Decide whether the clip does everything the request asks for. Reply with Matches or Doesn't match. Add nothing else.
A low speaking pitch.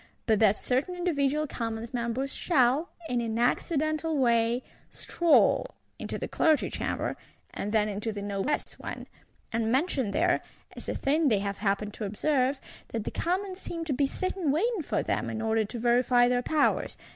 Doesn't match